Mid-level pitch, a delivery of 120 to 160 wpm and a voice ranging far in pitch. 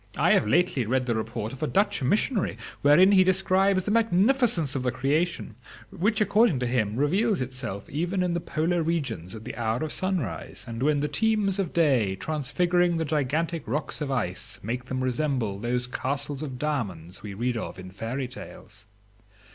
No: medium, 145 Hz; average, 180 wpm; wide, 6.8 semitones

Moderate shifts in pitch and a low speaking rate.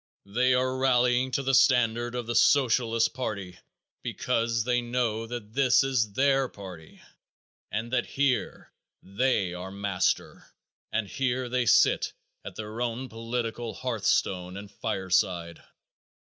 Yes: average, 3.6 semitones; slow, 130 wpm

